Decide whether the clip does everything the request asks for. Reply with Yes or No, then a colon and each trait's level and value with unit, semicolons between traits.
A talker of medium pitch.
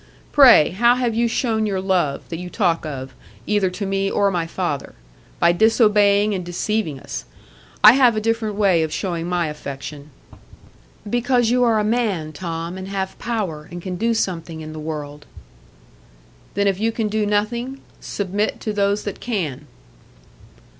No: high, 195 Hz